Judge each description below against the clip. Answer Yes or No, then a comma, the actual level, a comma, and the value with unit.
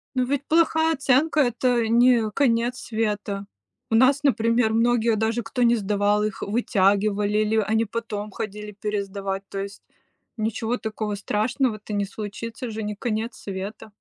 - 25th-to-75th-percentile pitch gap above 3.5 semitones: No, narrow, 2.6 semitones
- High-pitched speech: Yes, high, 220 Hz